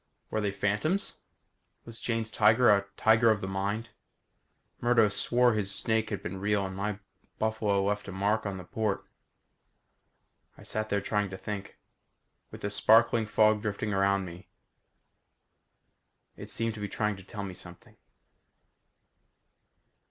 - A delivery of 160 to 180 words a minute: No, average, 145 wpm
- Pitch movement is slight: Yes, narrow, 2.0 semitones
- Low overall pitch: Yes, low, 105 Hz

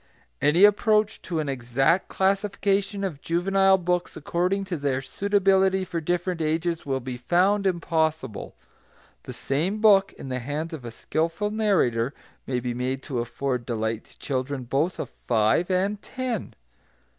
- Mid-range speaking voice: Yes, medium, 170 Hz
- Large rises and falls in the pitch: Yes, wide, 6.5 semitones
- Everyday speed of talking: Yes, average, 150 wpm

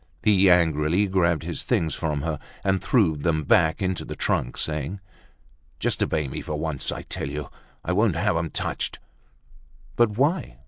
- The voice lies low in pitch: Yes, very low, 85 Hz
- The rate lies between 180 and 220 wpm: No, average, 170 wpm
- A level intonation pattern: No, average, 4.1 semitones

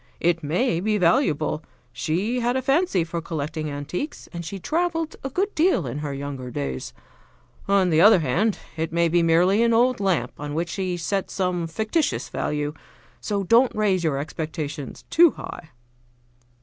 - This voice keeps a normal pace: Yes, average, 165 wpm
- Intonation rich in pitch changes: Yes, wide, 6.0 semitones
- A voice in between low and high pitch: Yes, medium, 175 Hz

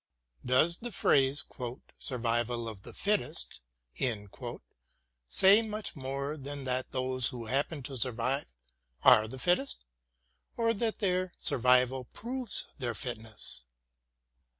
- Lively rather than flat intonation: Yes, wide, 6.5 semitones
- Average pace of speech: No, slow, 110 wpm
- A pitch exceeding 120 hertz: Yes, low, 135 Hz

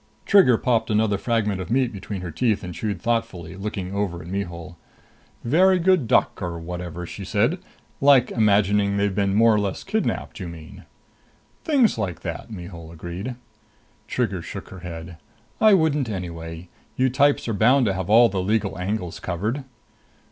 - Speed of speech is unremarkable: Yes, average, 165 wpm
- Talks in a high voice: No, low, 100 Hz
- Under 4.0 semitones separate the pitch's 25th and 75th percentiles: No, average, 4.8 semitones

